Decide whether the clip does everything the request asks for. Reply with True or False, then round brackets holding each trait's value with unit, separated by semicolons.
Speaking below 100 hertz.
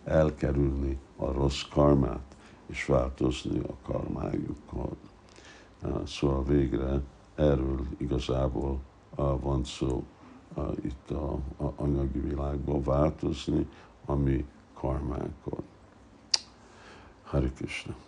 True (70 Hz)